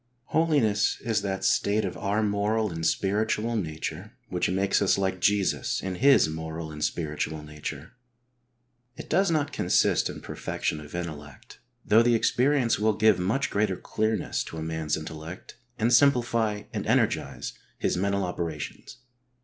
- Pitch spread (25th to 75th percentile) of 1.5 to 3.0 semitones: No, wide, 5.4 semitones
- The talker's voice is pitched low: Yes, low, 100 Hz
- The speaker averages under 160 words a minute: Yes, average, 150 wpm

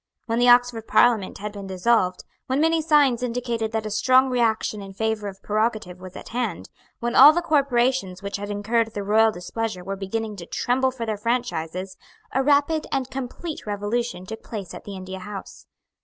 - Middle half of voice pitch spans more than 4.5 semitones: No, average, 3.8 semitones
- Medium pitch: No, high, 225 Hz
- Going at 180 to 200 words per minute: Yes, average, 185 wpm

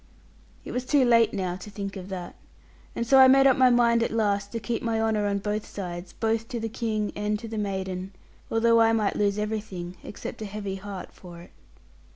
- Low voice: No, high, 210 Hz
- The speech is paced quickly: Yes, fast, 215 wpm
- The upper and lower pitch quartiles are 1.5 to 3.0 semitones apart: Yes, average, 2.7 semitones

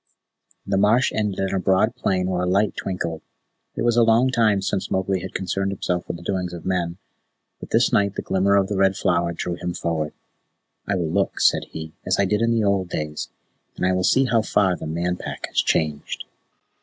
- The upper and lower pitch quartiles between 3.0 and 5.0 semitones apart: No, narrow, 2.4 semitones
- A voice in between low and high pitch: No, very low, 95 Hz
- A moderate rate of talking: No, fast, 220 wpm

